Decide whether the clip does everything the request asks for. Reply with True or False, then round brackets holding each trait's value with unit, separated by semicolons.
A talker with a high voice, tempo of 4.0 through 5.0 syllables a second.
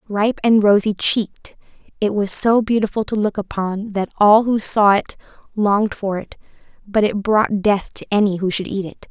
True (205 Hz; 4.8 syllables/s)